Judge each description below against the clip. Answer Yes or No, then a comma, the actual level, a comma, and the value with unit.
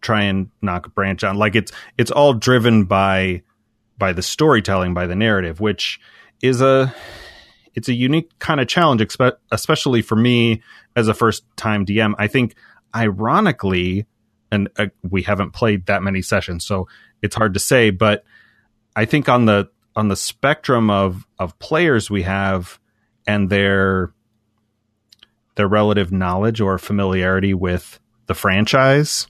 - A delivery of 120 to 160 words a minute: Yes, average, 155 wpm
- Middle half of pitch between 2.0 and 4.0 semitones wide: Yes, average, 2.7 semitones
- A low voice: Yes, low, 105 Hz